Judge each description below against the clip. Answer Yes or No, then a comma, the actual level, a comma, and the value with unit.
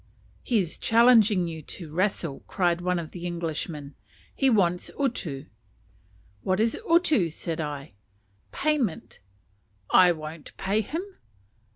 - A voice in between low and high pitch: Yes, medium, 180 Hz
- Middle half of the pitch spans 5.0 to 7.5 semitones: Yes, wide, 5.6 semitones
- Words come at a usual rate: No, slow, 125 wpm